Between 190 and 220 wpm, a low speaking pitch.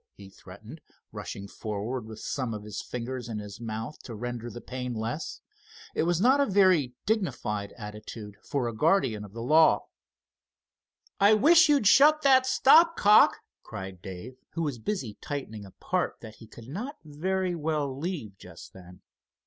No: average, 165 wpm; low, 125 Hz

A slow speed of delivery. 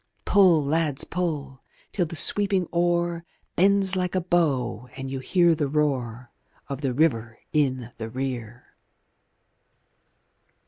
Yes: slow, 125 wpm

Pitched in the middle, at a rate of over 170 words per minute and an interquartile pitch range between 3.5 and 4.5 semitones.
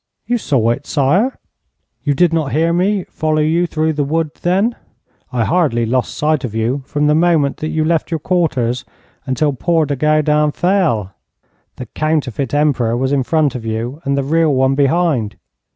Yes: medium, 150 Hz; average, 180 wpm; average, 3.9 semitones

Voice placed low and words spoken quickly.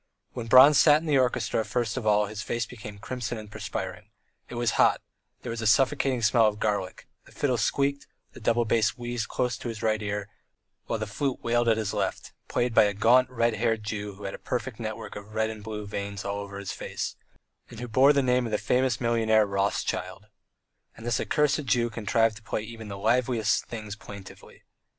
Yes: low, 110 Hz; fast, 210 wpm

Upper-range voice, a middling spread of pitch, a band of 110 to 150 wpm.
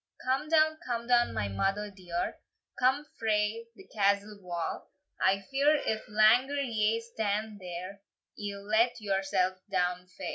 Yes: high, 210 Hz; average, 3.6 semitones; average, 140 wpm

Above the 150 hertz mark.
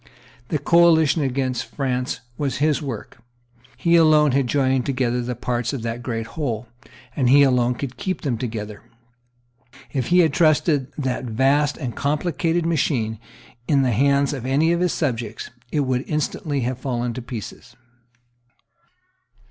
No: low, 135 Hz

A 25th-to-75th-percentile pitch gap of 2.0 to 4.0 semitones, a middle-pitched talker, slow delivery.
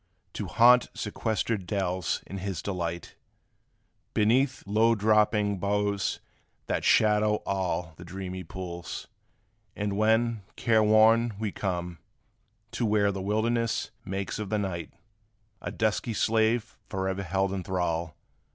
No: average, 2.7 semitones; low, 100 Hz; slow, 125 wpm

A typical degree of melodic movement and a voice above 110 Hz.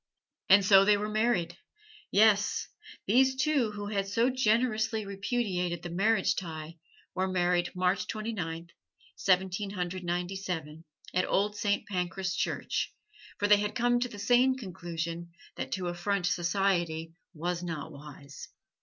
Yes: average, 3.4 semitones; high, 190 Hz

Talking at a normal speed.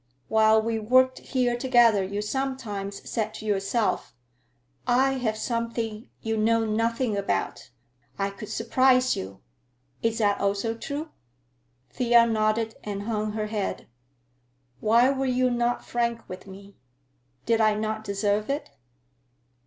No: slow, 130 wpm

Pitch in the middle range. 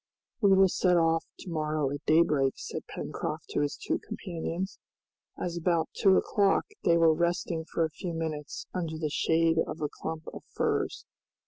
Yes: medium, 165 Hz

